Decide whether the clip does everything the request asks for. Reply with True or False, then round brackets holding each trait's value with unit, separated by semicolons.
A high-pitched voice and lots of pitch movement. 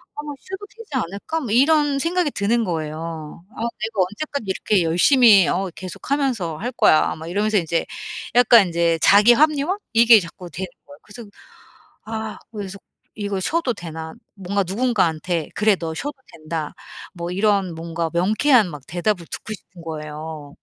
True (195 Hz; 6.1 semitones)